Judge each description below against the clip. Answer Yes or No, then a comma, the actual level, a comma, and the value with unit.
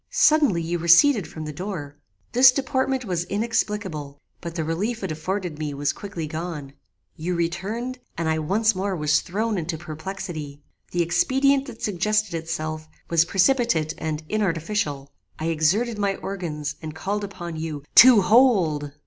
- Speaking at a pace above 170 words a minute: No, average, 150 wpm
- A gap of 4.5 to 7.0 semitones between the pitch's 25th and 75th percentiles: Yes, average, 5.2 semitones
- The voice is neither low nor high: Yes, medium, 175 Hz